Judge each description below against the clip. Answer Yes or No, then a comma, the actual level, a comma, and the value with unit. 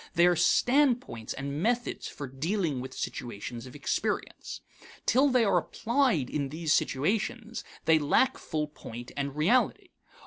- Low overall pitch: No, medium, 160 Hz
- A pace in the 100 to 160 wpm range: Yes, average, 140 wpm